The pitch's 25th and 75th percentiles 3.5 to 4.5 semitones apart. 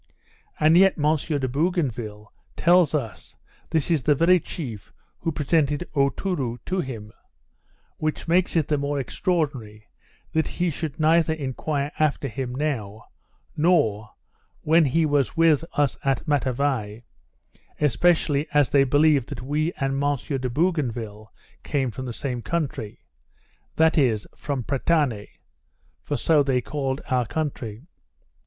Yes: average, 4.0 semitones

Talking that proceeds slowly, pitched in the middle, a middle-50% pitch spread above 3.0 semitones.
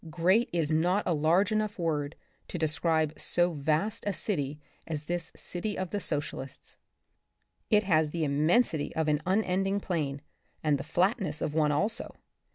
No: average, 160 wpm; medium, 165 Hz; average, 4.2 semitones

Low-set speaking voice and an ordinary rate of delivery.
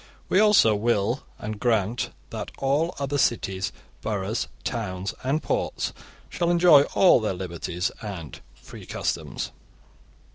No: low, 115 Hz; slow, 120 wpm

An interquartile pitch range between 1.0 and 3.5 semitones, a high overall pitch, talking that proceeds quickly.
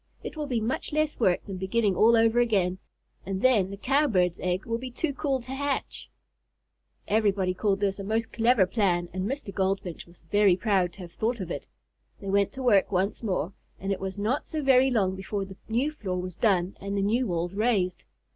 No: average, 4.3 semitones; high, 200 Hz; fast, 210 wpm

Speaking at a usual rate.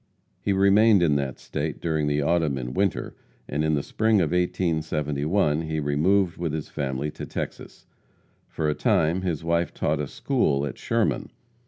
Yes: average, 170 wpm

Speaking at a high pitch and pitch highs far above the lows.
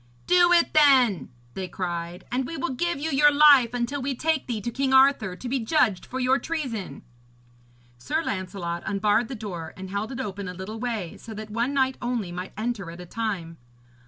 Yes: high, 235 Hz; wide, 6.0 semitones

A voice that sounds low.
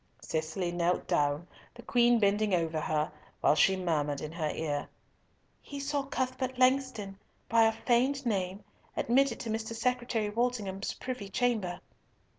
No: high, 215 Hz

